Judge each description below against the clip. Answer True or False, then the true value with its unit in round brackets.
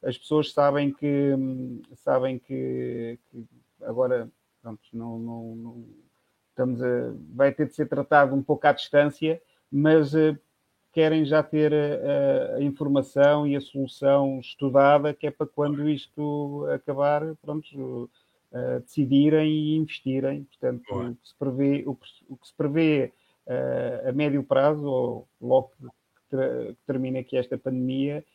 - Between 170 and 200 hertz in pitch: False (140 Hz)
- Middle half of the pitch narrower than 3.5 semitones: True (2.7 semitones)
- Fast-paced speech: False (145 wpm)